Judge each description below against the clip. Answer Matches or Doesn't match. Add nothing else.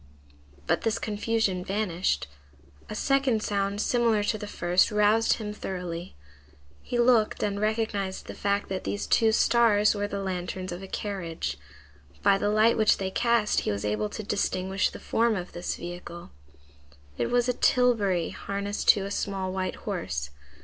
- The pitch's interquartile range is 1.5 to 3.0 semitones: Matches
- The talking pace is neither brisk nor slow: Matches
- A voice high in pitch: Matches